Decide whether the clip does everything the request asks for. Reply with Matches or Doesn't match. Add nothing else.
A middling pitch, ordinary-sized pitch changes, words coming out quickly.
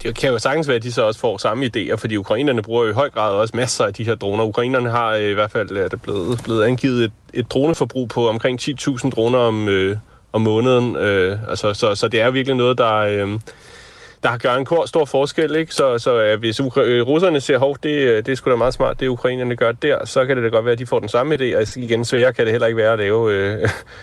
Doesn't match